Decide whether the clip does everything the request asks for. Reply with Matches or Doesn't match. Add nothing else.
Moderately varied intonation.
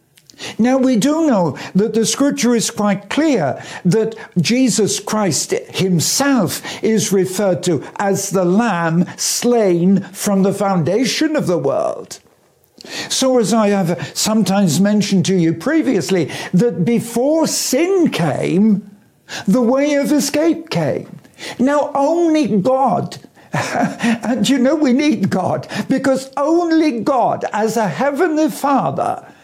Doesn't match